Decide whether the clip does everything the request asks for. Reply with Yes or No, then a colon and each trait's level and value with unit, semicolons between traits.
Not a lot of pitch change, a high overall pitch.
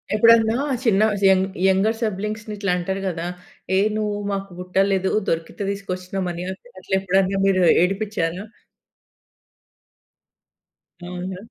Yes: narrow, 2.2 semitones; high, 195 Hz